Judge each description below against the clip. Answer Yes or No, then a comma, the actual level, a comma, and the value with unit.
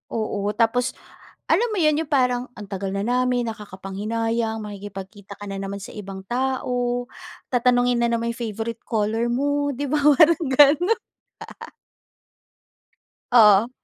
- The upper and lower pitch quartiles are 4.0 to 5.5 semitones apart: No, average, 3.5 semitones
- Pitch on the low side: No, high, 235 Hz